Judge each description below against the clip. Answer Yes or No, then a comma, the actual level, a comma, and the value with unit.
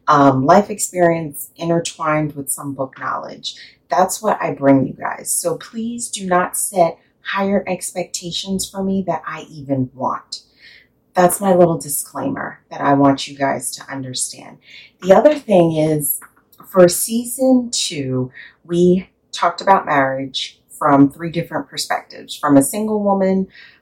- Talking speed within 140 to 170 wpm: Yes, average, 145 wpm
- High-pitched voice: No, medium, 170 Hz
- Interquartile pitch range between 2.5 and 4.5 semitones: No, wide, 5.4 semitones